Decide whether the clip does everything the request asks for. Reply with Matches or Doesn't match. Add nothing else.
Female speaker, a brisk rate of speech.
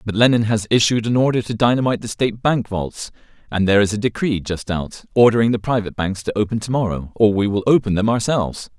Doesn't match